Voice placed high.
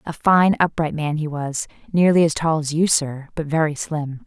No: medium, 155 Hz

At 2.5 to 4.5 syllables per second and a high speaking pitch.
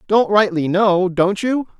Yes: 3.9 syllables/s; high, 195 Hz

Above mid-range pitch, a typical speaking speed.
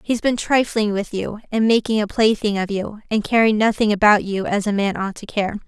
No: high, 210 Hz; fast, 235 wpm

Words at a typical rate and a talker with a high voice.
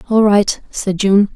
Yes: average, 175 wpm; high, 200 Hz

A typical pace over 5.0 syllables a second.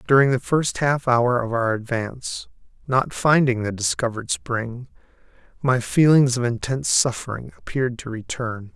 No: 4.8 syllables/s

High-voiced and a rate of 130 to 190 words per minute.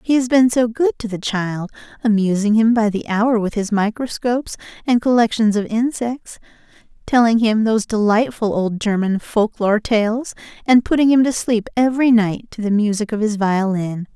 Yes: high, 220 Hz; average, 180 wpm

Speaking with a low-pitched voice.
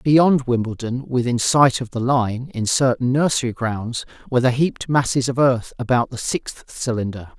Yes: low, 125 Hz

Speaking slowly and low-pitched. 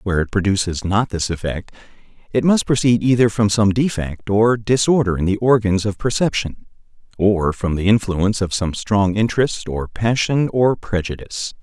No: average, 165 wpm; low, 105 Hz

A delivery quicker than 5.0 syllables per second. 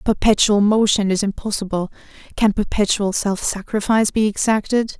Yes: 5.4 syllables/s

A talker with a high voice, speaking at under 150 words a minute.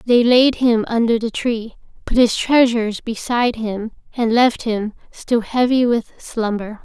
No: high, 230 Hz; average, 160 wpm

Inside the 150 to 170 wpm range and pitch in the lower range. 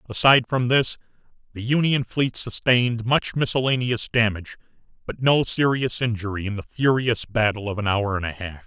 Yes: average, 165 wpm; low, 115 Hz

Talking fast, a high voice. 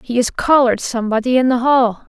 No: average, 190 wpm; high, 245 Hz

